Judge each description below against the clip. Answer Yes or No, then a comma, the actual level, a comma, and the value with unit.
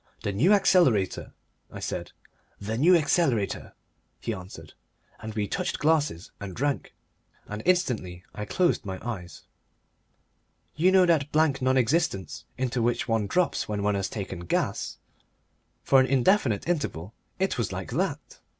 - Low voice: Yes, low, 120 Hz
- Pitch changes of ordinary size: No, wide, 7.7 semitones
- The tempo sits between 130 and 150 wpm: Yes, average, 145 wpm